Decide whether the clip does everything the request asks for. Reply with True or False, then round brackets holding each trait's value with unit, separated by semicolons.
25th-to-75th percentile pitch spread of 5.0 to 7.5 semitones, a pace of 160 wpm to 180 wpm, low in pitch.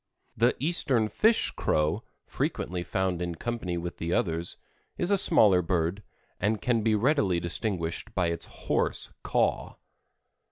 False (5.6 semitones; 135 wpm; 95 Hz)